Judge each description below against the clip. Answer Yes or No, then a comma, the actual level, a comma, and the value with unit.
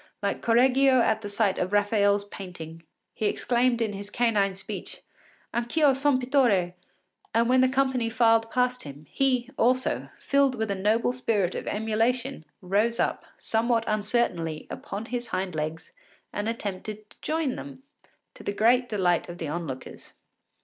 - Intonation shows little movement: No, average, 4.0 semitones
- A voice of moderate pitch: No, high, 225 Hz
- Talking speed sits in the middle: Yes, average, 155 wpm